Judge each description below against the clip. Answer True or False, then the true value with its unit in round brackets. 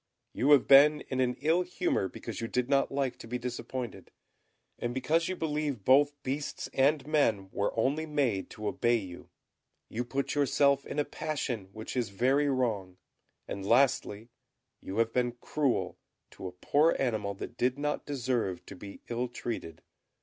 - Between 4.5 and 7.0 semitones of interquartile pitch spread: False (4.1 semitones)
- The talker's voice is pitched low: True (125 Hz)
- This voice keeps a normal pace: True (170 wpm)